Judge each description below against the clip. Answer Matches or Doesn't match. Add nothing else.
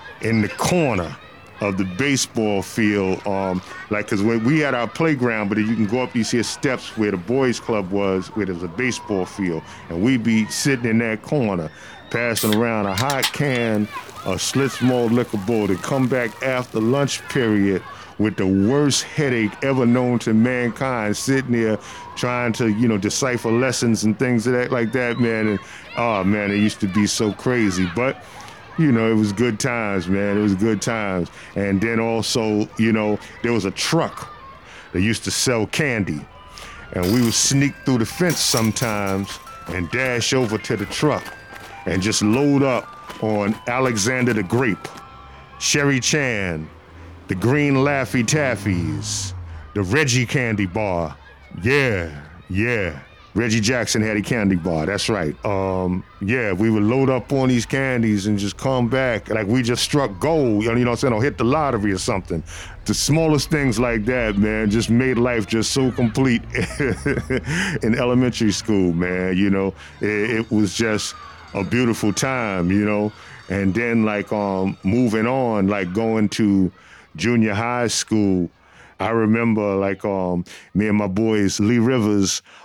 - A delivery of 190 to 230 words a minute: Doesn't match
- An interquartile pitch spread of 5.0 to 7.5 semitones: Doesn't match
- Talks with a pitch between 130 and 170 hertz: Doesn't match